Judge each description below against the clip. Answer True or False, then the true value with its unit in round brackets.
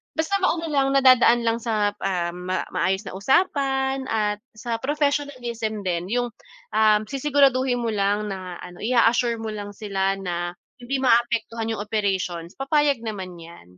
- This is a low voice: False (225 Hz)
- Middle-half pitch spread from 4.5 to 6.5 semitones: True (5.0 semitones)